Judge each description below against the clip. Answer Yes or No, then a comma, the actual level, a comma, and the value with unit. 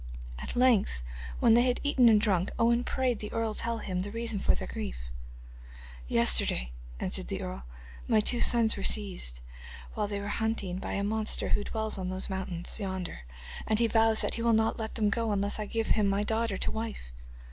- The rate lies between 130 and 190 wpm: No, fast, 205 wpm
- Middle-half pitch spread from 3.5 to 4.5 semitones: No, average, 3.1 semitones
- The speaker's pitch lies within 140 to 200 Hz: No, high, 215 Hz